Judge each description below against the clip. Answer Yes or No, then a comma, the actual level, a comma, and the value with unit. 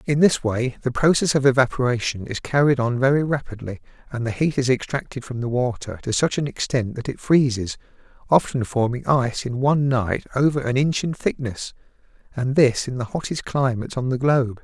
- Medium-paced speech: Yes, average, 195 wpm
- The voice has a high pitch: No, low, 130 Hz